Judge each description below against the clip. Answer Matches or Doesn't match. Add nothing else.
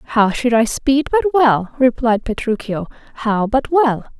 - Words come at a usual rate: Matches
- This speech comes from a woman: Matches